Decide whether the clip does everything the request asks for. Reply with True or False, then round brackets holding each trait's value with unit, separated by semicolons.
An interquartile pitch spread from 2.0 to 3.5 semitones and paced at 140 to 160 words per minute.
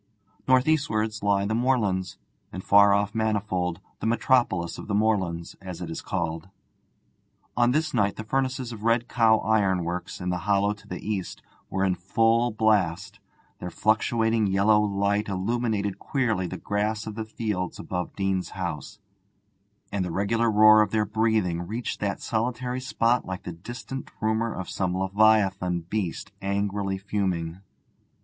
True (3.1 semitones; 155 wpm)